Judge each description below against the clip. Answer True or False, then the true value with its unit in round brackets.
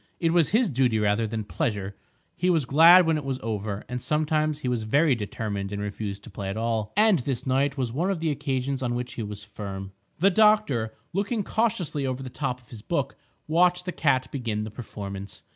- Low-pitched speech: True (130 Hz)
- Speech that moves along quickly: True (210 wpm)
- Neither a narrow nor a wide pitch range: False (6.7 semitones)